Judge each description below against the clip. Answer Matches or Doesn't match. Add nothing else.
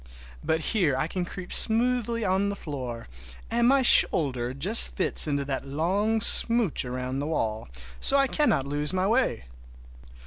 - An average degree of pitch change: Doesn't match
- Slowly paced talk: Doesn't match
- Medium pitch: Matches